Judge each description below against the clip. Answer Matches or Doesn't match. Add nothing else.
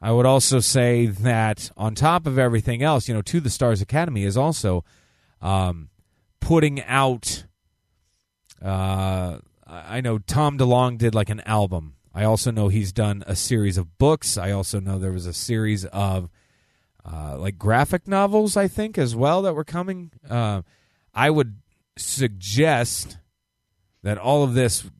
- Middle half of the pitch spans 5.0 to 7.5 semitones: Matches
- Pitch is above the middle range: Doesn't match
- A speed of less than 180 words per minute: Matches